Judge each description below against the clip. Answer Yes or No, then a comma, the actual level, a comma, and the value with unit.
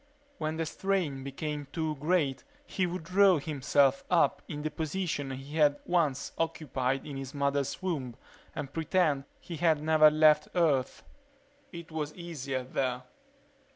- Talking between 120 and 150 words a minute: Yes, average, 145 wpm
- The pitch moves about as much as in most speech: Yes, average, 3.1 semitones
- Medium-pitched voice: Yes, medium, 150 Hz